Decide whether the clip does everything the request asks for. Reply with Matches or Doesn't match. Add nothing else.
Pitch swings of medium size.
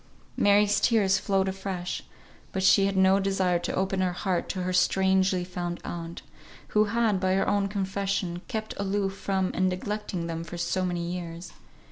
Doesn't match